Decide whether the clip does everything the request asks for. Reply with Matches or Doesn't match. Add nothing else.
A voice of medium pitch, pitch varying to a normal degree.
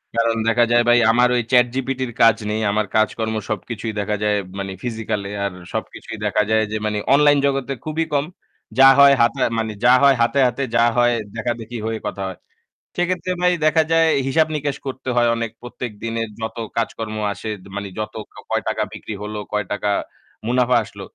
Doesn't match